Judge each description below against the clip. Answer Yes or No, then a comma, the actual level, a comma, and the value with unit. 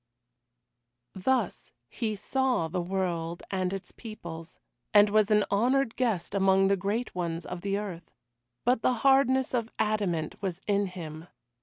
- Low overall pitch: No, high, 200 Hz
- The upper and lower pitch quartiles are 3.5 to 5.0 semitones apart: Yes, average, 4.2 semitones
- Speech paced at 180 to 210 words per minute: No, average, 145 wpm